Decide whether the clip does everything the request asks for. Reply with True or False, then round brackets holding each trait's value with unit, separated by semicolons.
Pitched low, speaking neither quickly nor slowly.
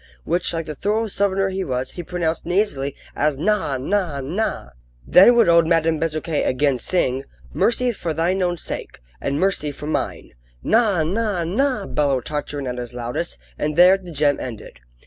False (165 Hz; 170 wpm)